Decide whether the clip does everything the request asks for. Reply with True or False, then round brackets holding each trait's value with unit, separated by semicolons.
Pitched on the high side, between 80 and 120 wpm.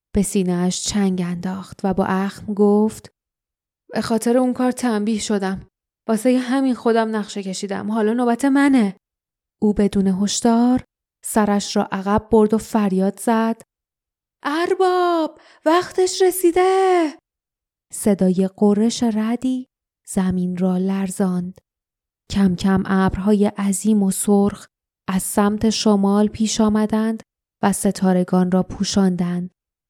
True (210 Hz; 110 wpm)